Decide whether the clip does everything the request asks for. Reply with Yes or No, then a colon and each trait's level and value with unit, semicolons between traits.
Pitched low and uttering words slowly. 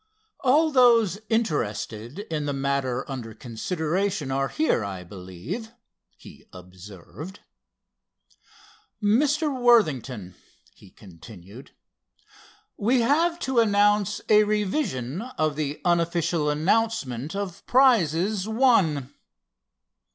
No: medium, 170 Hz; slow, 90 wpm